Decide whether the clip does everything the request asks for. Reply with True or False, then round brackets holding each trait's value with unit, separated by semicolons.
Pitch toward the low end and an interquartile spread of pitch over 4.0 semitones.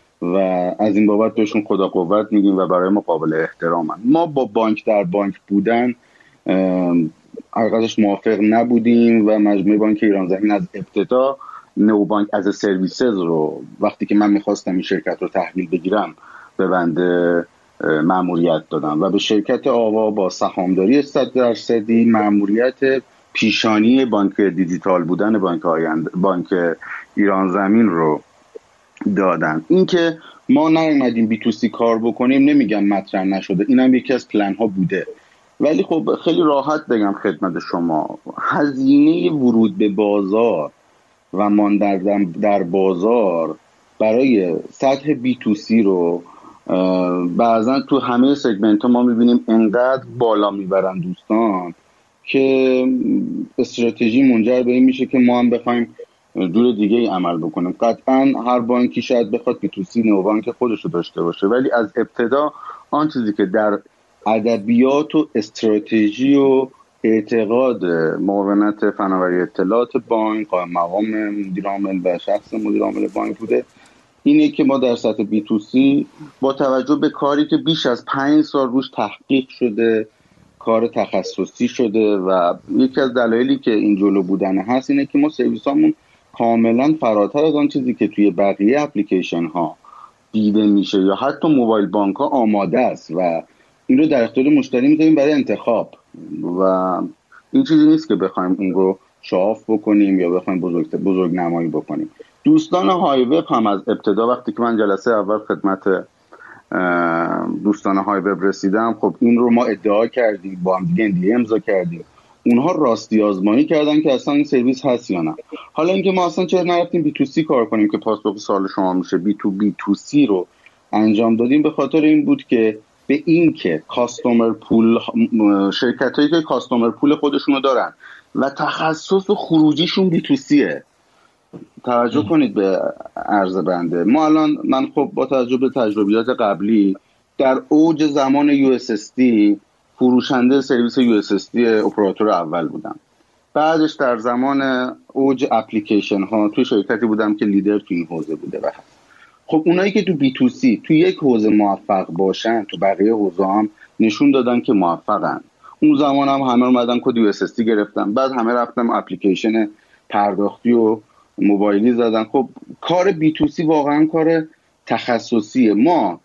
True (115 Hz; 5.2 semitones)